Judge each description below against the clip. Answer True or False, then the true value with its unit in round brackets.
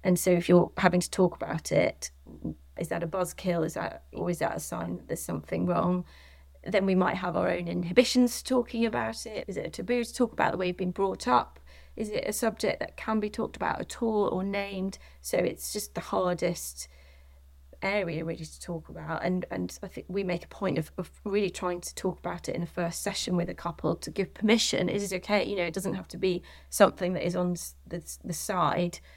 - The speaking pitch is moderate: True (175 Hz)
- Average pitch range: False (6.2 semitones)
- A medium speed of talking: False (235 wpm)